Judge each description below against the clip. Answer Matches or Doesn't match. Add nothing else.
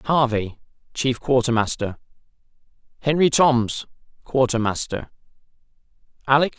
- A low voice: Matches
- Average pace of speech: Doesn't match